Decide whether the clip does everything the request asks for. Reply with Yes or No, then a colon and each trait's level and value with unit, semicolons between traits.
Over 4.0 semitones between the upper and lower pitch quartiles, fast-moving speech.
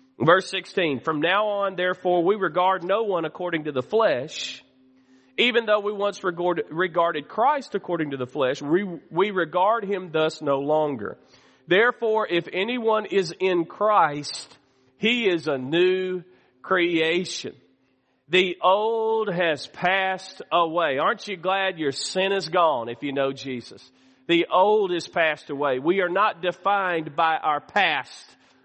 No: average, 4.5 semitones; average, 150 wpm